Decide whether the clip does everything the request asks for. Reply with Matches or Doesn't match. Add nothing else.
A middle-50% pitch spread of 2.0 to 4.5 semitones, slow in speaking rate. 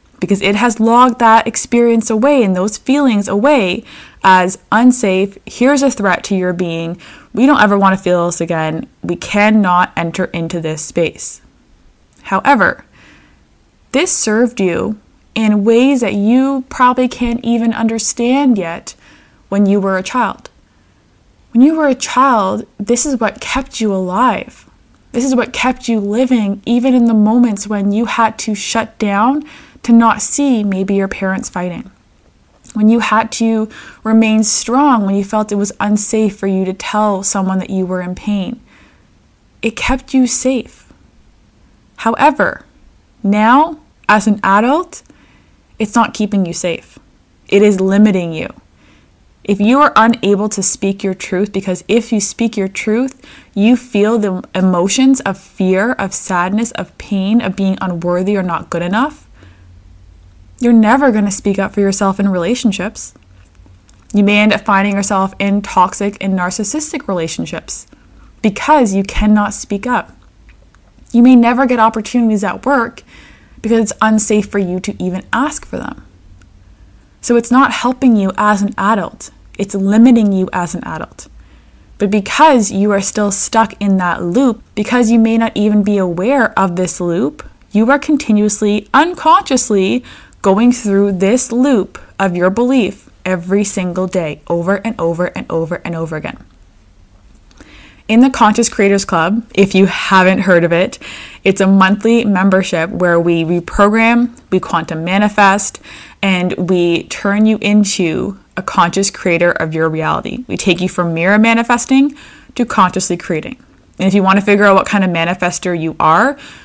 Doesn't match